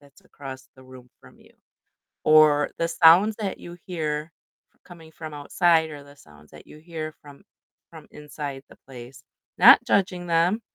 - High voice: No, medium, 155 Hz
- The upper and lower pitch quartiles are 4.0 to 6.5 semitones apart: No, average, 3.3 semitones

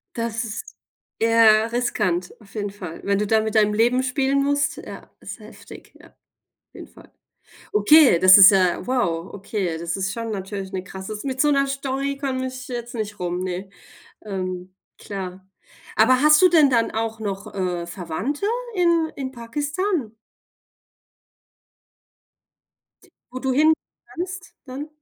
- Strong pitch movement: Yes, wide, 5.8 semitones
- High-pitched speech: Yes, high, 225 Hz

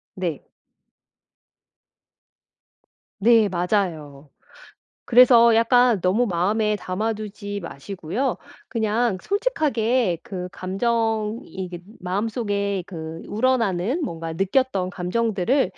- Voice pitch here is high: Yes, high, 205 Hz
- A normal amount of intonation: Yes, average, 4.3 semitones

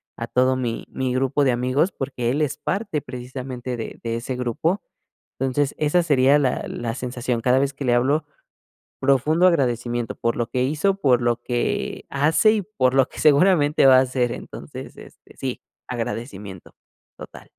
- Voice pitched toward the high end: No, low, 130 Hz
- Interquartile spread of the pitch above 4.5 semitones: No, average, 3.0 semitones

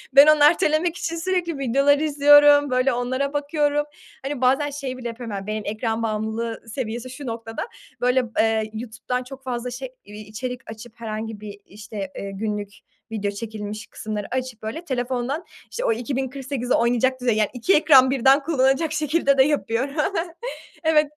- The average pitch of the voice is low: No, very high, 255 Hz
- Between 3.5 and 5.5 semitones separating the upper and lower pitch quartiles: Yes, average, 4.3 semitones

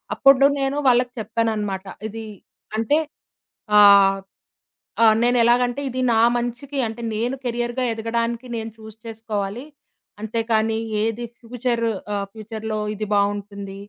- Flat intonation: Yes, narrow, 2.1 semitones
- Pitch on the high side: Yes, high, 225 Hz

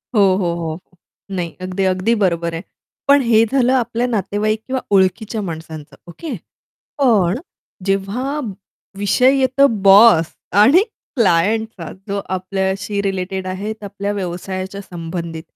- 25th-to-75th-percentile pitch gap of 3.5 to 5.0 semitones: Yes, average, 3.8 semitones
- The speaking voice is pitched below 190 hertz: No, high, 195 Hz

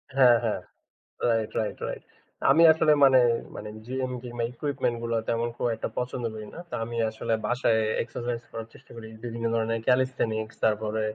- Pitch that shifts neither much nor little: No, narrow, 2.0 semitones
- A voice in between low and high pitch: No, low, 115 Hz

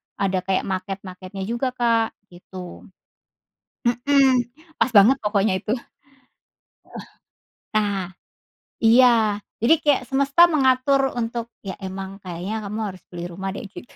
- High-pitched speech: Yes, high, 220 Hz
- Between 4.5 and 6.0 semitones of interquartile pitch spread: Yes, average, 4.8 semitones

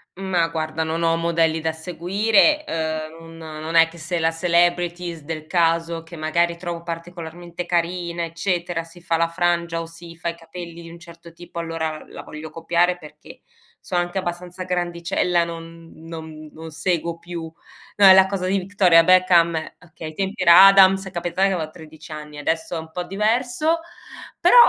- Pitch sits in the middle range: Yes, medium, 170 Hz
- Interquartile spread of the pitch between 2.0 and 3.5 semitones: No, narrow, 1.4 semitones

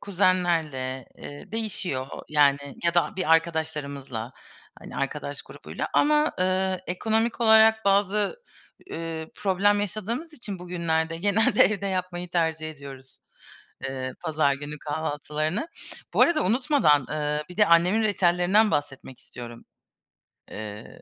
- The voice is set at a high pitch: No, medium, 170 Hz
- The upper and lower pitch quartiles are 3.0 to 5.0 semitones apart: No, wide, 5.6 semitones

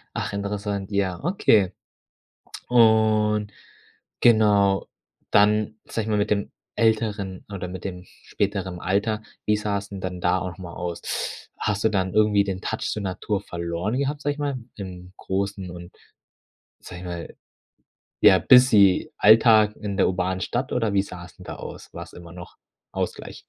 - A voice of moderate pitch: No, low, 100 Hz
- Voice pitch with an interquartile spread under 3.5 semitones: Yes, narrow, 2.6 semitones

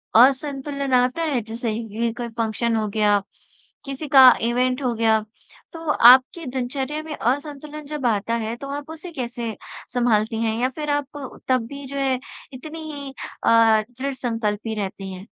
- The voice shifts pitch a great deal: No, average, 3.6 semitones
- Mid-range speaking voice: No, very high, 255 Hz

